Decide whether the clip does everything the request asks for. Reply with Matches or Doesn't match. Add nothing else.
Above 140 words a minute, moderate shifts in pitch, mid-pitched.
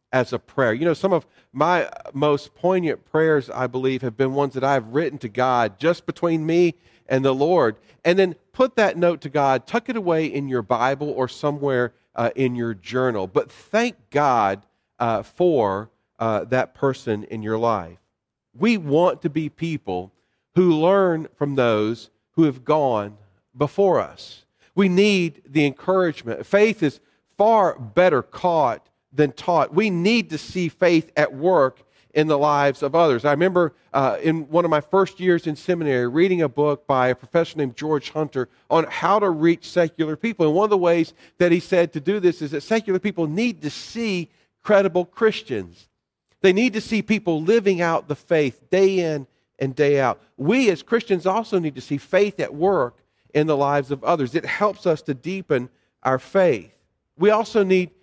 Doesn't match